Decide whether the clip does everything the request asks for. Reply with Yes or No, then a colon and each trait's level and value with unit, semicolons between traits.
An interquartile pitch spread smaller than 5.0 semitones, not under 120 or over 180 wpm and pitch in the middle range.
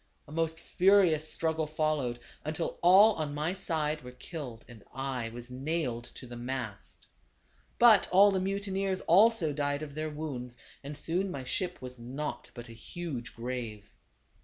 No: wide, 5.6 semitones; average, 160 wpm; medium, 150 Hz